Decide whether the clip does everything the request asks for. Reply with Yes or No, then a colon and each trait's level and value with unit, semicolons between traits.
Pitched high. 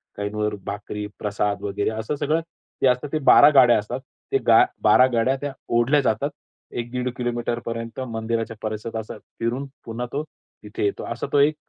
No: low, 120 Hz